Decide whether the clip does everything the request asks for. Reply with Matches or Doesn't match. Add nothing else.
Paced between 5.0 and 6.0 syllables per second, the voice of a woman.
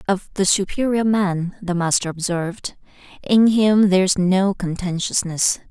Doesn't match